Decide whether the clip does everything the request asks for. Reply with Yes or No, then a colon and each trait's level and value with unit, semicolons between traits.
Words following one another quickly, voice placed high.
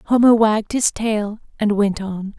No: average, 175 wpm; high, 215 Hz